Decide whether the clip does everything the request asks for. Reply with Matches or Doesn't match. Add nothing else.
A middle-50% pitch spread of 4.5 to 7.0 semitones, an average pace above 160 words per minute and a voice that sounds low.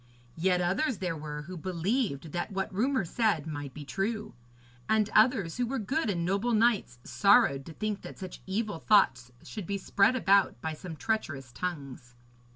Doesn't match